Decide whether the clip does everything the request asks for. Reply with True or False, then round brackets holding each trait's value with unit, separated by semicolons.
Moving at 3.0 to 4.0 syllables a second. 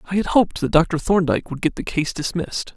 False (6.3 syllables/s)